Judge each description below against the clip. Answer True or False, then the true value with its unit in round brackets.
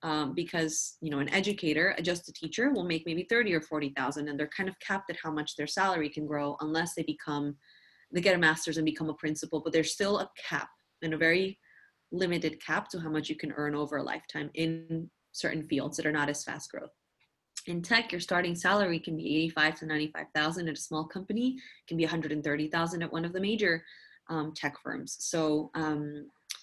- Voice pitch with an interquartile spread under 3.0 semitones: True (2.5 semitones)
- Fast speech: True (225 wpm)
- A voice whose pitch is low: False (160 Hz)